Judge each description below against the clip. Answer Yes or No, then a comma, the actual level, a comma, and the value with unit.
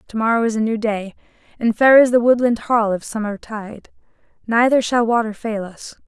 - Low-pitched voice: No, high, 225 Hz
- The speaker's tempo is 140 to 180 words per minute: No, average, 200 wpm